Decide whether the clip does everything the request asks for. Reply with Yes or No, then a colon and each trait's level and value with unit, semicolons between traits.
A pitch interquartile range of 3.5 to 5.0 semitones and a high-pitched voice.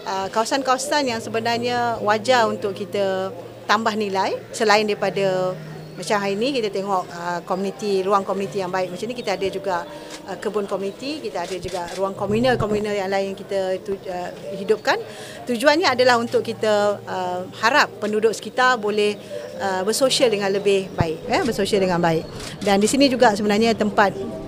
No: average, 2.9 semitones; high, 205 Hz